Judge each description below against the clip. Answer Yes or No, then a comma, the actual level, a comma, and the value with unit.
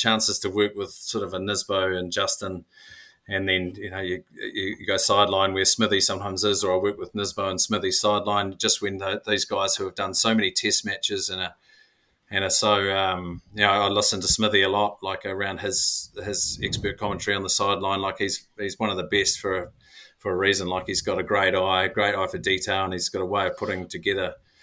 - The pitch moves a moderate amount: No, narrow, 1.3 semitones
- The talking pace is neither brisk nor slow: No, fast, 235 wpm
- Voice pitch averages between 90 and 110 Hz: Yes, low, 100 Hz